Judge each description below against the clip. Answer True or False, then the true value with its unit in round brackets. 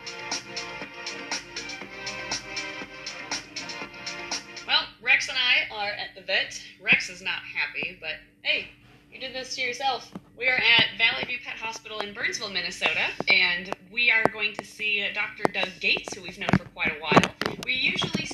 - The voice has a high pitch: True (220 Hz)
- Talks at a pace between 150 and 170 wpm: True (155 wpm)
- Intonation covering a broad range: False (3.4 semitones)